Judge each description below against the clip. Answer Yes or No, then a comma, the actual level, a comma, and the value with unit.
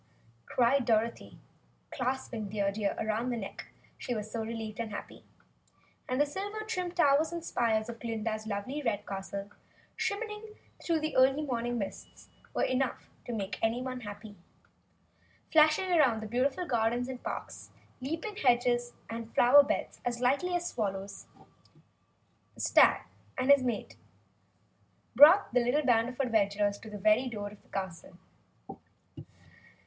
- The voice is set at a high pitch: Yes, high, 240 Hz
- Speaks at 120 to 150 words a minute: Yes, average, 145 wpm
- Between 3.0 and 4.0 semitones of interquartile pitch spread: No, average, 4.5 semitones